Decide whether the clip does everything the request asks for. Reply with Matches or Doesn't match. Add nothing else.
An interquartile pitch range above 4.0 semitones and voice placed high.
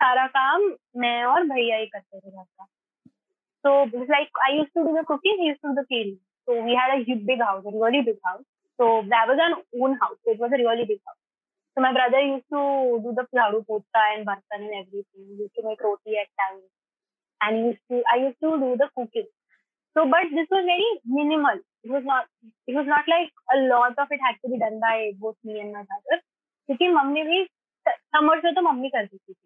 Matches